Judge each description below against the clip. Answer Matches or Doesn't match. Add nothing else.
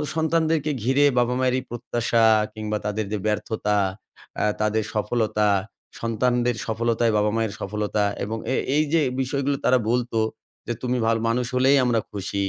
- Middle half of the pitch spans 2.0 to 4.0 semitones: Matches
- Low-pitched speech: Matches